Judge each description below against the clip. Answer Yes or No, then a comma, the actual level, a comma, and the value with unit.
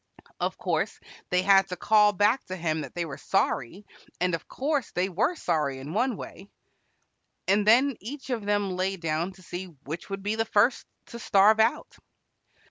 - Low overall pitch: No, high, 195 Hz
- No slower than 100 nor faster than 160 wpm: No, average, 185 wpm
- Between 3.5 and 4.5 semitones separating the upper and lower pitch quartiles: Yes, average, 3.8 semitones